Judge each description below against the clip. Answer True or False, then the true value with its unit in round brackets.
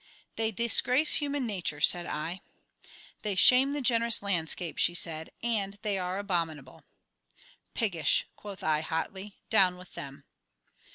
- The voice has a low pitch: False (195 Hz)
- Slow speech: True (130 wpm)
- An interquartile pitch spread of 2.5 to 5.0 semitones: False (5.4 semitones)